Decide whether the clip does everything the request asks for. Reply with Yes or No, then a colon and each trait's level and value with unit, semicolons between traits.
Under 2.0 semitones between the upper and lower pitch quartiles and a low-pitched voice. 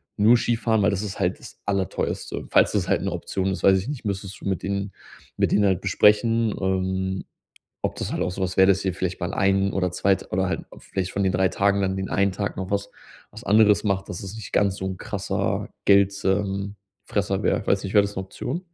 Yes: narrow, 1.2 semitones; low, 100 Hz